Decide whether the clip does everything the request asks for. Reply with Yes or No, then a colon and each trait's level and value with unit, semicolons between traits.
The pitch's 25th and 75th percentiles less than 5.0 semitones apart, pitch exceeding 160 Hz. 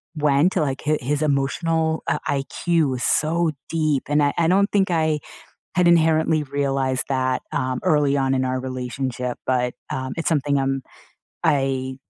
No: average, 3.3 semitones; medium, 140 Hz